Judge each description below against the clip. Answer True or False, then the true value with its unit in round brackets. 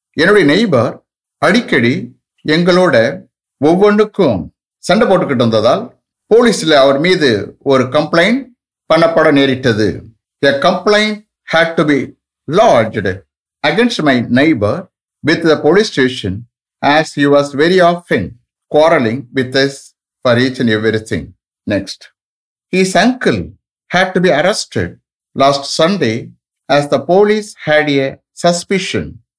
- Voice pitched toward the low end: False (150 Hz)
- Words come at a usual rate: False (75 wpm)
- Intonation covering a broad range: True (6.2 semitones)